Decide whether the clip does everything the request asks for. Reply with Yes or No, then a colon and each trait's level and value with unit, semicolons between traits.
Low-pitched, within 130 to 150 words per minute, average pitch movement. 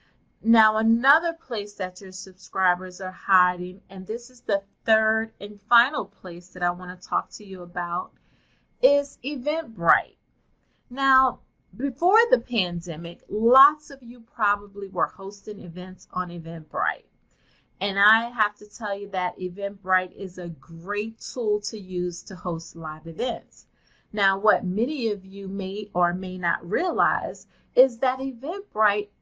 No: high, 200 Hz; average, 145 wpm; average, 3.9 semitones